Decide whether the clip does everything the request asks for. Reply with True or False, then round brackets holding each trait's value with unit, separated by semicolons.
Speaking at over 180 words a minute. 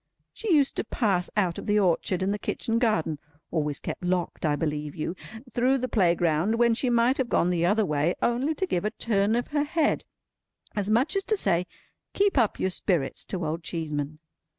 True (200 wpm)